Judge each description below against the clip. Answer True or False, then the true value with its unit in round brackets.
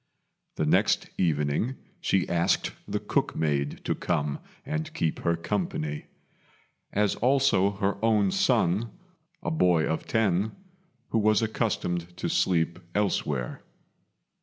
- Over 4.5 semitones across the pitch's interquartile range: True (4.9 semitones)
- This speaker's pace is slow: True (120 wpm)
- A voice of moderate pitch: False (95 Hz)